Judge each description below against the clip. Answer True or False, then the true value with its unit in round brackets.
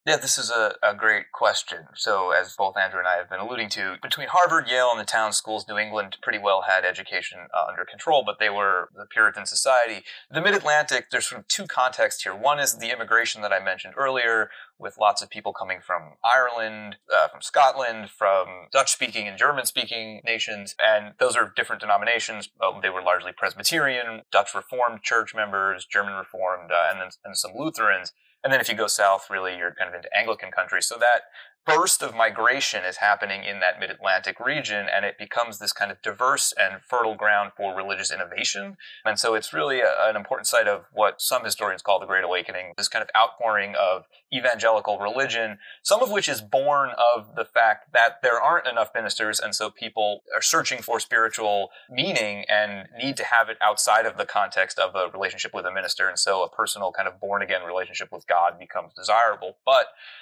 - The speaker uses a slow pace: False (200 wpm)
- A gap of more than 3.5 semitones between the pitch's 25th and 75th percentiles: False (2.9 semitones)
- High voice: False (110 Hz)